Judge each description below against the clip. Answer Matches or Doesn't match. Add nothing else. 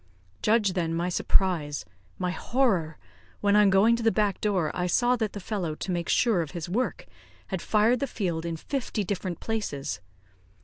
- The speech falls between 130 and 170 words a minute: Doesn't match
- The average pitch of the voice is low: Doesn't match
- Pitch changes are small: Doesn't match